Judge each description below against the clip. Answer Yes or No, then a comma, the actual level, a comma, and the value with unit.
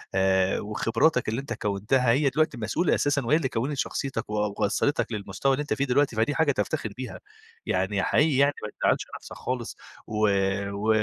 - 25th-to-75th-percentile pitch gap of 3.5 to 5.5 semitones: Yes, average, 4.9 semitones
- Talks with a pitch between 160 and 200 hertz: No, low, 120 Hz